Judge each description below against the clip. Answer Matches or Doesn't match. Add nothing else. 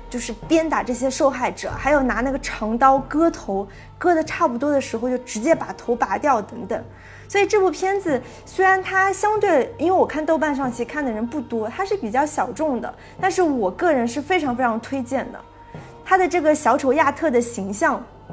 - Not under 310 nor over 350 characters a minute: Doesn't match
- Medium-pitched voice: Doesn't match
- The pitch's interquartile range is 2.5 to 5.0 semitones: Doesn't match